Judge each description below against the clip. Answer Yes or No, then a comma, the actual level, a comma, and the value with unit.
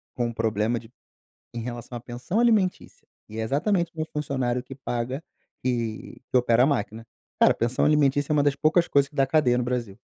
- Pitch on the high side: No, low, 125 Hz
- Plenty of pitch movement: No, average, 3.8 semitones